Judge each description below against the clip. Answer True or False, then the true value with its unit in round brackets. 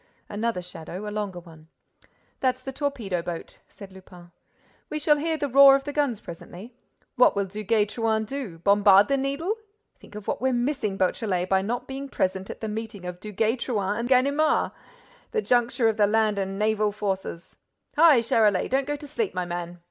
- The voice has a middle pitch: False (215 Hz)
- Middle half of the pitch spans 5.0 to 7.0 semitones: True (5.5 semitones)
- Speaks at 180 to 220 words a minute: True (185 wpm)